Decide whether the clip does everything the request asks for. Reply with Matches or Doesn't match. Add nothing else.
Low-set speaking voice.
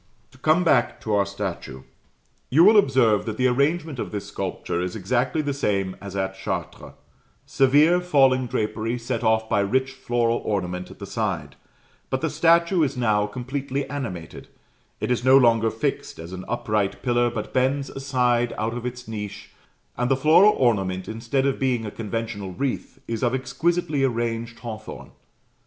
Matches